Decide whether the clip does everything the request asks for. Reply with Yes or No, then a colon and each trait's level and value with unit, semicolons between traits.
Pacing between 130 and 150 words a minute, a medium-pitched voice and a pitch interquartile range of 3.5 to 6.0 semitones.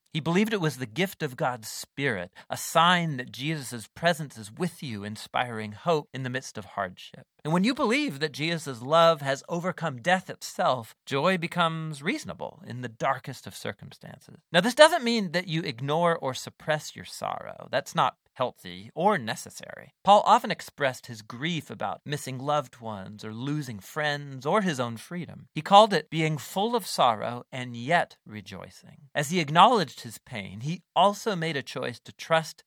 No: average, 180 wpm; medium, 155 Hz; average, 5.3 semitones